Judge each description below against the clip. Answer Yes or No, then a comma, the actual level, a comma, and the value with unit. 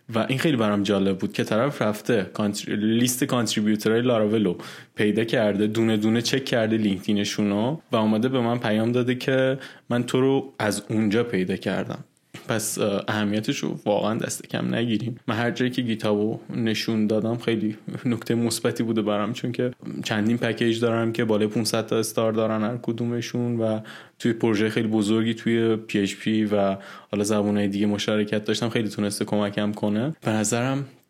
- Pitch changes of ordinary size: No, narrow, 2.0 semitones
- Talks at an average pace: No, fast, 165 wpm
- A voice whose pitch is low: Yes, low, 110 Hz